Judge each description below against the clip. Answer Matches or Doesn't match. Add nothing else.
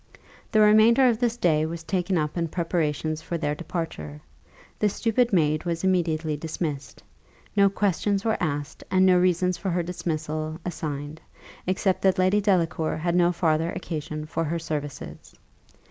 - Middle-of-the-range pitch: Matches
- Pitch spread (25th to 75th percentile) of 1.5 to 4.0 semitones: Matches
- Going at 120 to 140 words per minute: Doesn't match